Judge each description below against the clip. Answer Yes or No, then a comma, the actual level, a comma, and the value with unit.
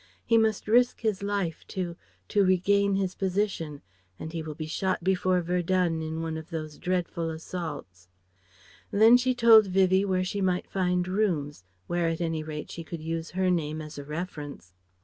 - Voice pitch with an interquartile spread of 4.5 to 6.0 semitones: No, average, 3.3 semitones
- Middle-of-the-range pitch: Yes, medium, 180 Hz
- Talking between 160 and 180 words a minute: Yes, average, 175 wpm